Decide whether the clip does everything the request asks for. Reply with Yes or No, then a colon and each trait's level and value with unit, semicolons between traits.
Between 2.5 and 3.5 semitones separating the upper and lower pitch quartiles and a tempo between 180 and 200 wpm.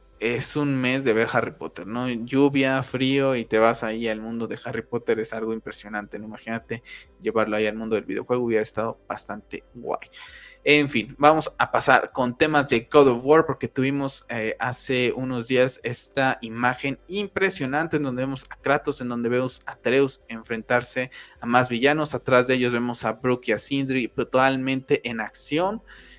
Yes: average, 3.0 semitones; average, 185 wpm